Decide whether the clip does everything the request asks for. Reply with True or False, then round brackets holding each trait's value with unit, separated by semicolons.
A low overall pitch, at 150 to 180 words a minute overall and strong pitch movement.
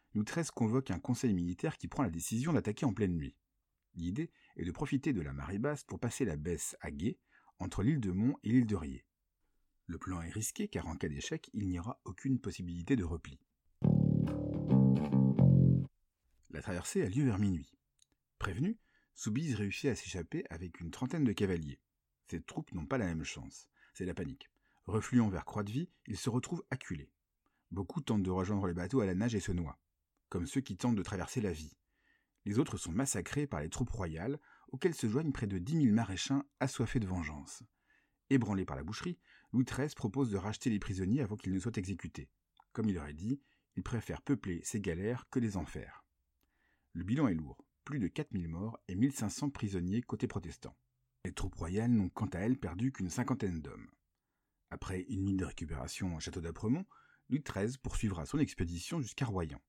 False (105 Hz; 190 wpm; 6.5 semitones)